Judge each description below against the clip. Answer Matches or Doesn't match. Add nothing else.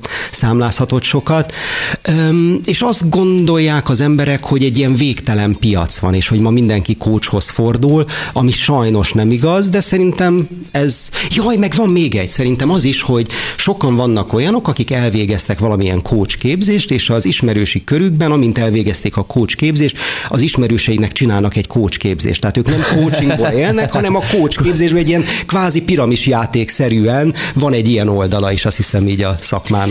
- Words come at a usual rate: Doesn't match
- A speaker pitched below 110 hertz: Doesn't match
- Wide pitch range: Matches